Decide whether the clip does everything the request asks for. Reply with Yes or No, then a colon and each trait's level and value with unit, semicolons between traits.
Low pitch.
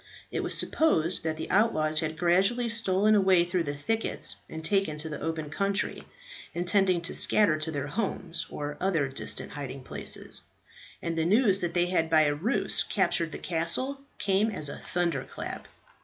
No: medium, 170 Hz